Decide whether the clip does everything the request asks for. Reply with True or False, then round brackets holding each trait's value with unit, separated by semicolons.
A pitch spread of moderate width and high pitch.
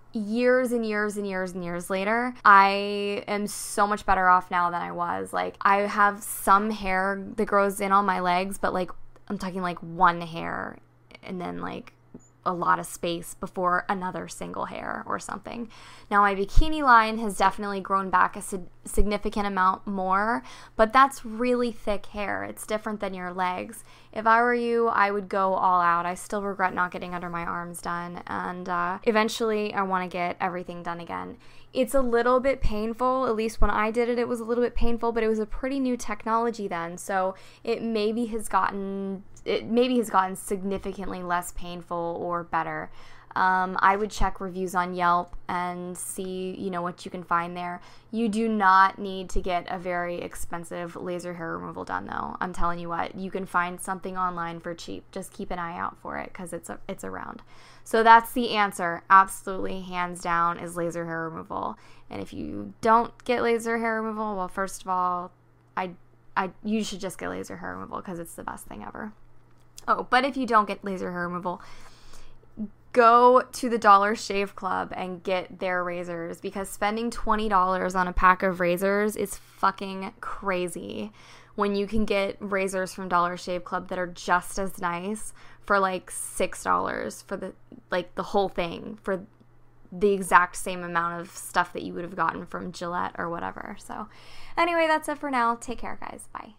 True (3.3 semitones; 195 Hz)